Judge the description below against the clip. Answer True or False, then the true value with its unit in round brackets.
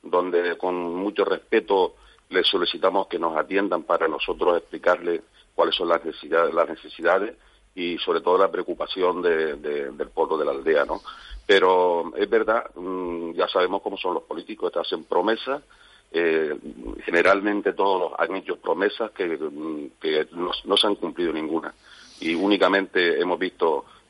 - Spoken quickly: False (150 wpm)